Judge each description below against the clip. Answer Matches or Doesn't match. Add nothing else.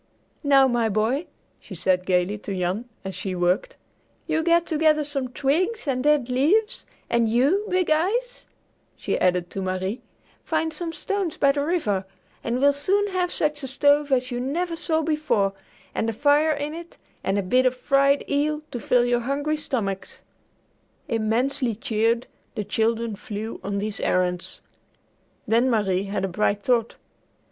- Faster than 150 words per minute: Matches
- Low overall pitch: Doesn't match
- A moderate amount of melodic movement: Doesn't match